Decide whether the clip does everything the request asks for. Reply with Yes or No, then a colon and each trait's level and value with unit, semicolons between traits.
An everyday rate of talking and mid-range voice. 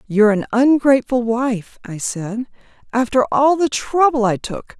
No: average, 150 wpm; high, 245 Hz